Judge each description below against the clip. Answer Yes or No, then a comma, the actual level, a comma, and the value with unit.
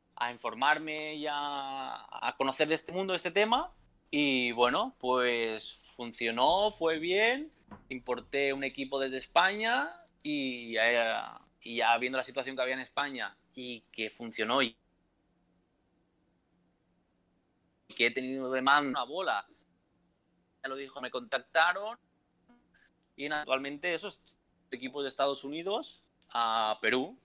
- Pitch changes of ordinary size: Yes, average, 3.9 semitones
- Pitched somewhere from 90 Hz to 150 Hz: Yes, low, 135 Hz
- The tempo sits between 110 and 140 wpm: Yes, average, 130 wpm